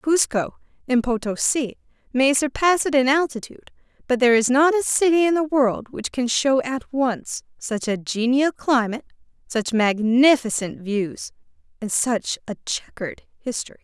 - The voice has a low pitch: No, very high, 255 Hz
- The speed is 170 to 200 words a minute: No, average, 145 wpm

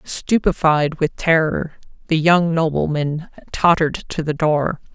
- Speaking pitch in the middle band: Yes, medium, 160 Hz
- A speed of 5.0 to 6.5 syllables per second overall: No, 4.0 syllables/s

